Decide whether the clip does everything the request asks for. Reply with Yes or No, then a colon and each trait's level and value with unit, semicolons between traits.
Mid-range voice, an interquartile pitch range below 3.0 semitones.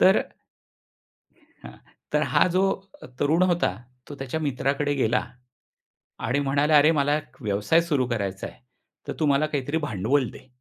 No: medium, 145 Hz; average, 3.3 semitones